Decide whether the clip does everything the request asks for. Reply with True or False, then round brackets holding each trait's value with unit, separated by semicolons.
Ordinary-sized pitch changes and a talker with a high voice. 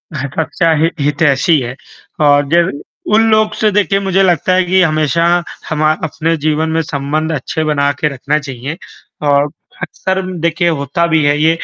False (3.1 semitones; 155 Hz)